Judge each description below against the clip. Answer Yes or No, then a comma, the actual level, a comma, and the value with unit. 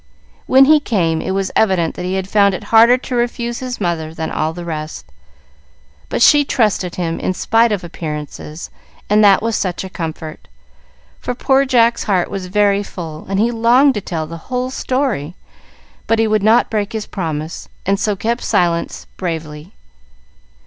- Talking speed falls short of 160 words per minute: No, average, 175 wpm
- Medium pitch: No, high, 195 Hz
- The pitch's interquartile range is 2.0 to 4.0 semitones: No, wide, 5.6 semitones